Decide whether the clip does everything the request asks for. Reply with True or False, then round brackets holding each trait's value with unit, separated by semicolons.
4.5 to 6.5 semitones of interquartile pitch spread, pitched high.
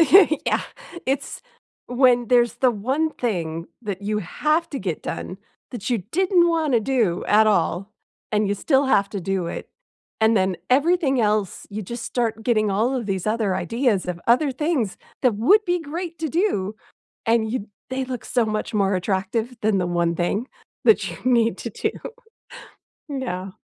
True (5.1 semitones; 230 Hz)